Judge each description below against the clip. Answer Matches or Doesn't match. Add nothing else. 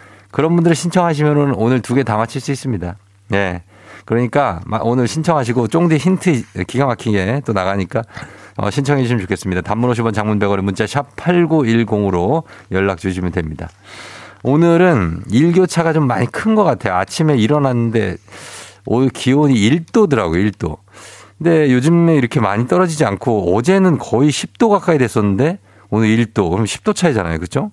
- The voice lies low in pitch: Matches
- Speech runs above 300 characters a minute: Matches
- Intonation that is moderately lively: Doesn't match